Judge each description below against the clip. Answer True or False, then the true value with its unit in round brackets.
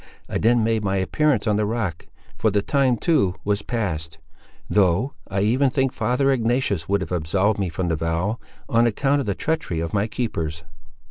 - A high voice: False (105 Hz)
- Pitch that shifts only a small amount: False (4.9 semitones)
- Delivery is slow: False (190 wpm)